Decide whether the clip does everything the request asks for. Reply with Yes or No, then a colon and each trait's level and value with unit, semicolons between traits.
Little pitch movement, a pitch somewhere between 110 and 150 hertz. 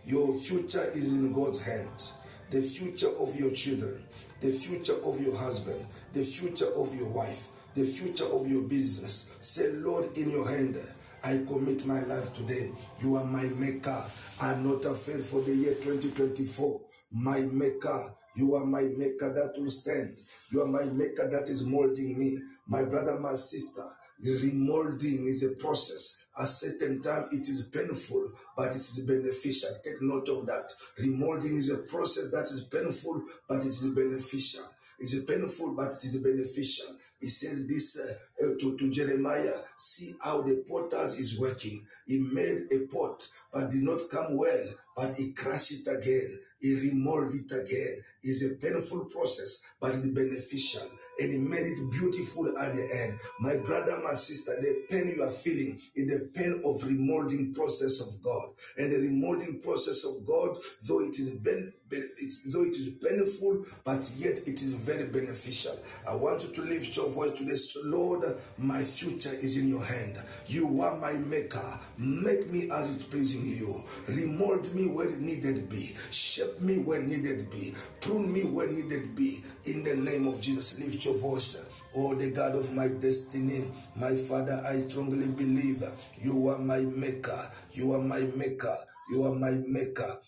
Yes: narrow, 1.7 semitones; low, 135 Hz